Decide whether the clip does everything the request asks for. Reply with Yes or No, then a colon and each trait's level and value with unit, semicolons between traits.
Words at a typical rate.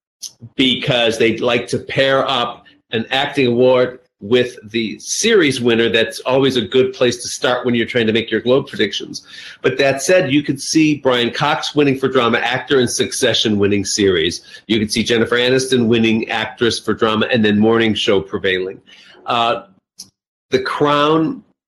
Yes: average, 170 wpm